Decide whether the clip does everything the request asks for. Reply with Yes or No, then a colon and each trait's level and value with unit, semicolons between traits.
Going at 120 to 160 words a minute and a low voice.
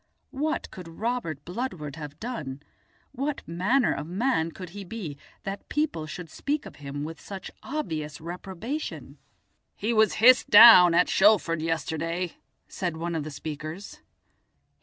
No: average, 140 wpm; medium, 180 Hz